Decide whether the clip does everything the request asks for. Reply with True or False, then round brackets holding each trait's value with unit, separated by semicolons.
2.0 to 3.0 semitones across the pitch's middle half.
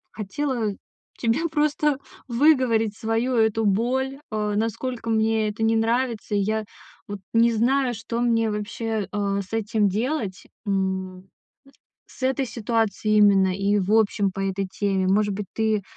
True (2.5 semitones)